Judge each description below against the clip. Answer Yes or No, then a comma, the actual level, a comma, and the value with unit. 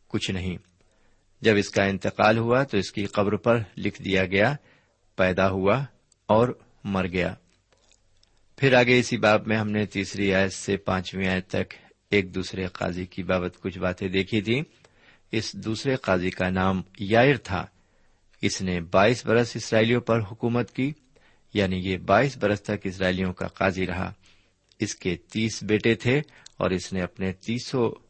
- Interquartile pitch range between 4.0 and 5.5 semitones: No, average, 3.1 semitones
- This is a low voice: Yes, low, 100 Hz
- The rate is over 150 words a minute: Yes, average, 165 wpm